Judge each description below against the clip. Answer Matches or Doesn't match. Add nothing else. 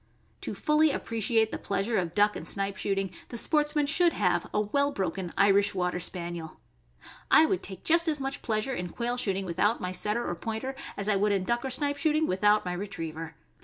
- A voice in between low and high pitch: Doesn't match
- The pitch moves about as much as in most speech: Doesn't match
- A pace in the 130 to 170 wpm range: Doesn't match